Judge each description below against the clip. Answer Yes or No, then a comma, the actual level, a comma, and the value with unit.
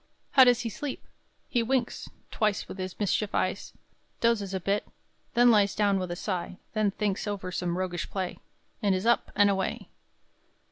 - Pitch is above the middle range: Yes, high, 205 Hz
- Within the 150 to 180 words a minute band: Yes, average, 175 wpm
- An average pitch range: Yes, average, 3.3 semitones